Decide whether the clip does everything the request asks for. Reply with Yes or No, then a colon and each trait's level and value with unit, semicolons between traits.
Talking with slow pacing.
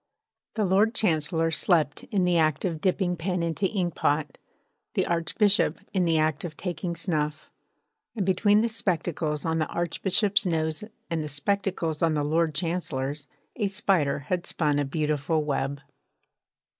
No: average, 150 wpm